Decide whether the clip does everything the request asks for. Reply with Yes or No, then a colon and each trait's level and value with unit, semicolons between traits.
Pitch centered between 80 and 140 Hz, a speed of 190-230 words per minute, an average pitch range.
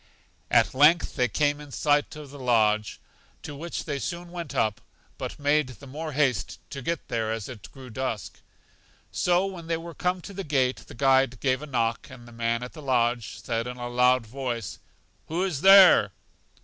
Yes: low, 135 Hz; average, 195 wpm; average, 4.4 semitones